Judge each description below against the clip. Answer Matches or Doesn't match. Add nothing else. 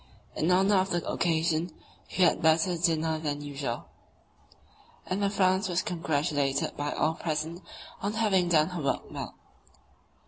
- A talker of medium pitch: Matches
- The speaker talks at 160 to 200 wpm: Doesn't match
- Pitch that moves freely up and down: Doesn't match